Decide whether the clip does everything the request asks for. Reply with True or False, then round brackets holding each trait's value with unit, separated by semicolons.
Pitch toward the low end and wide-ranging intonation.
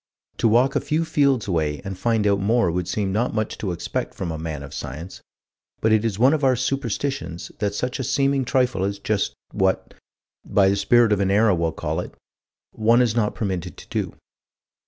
False (105 Hz; 4.5 semitones)